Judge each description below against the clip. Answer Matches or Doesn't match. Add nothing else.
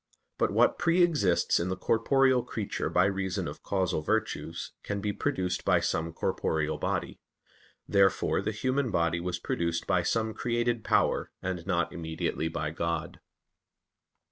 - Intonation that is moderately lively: Matches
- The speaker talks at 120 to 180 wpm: Matches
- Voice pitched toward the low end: Matches